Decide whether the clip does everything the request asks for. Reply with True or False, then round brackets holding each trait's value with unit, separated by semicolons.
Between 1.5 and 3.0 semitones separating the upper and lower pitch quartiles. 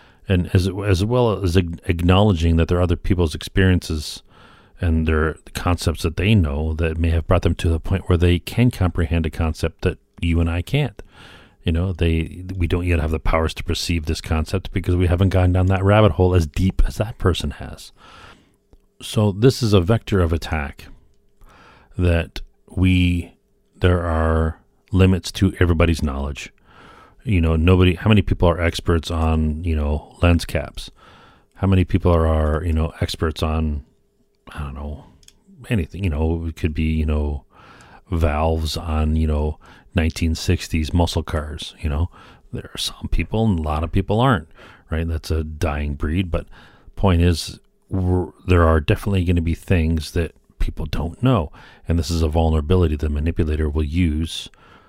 True (2.7 semitones)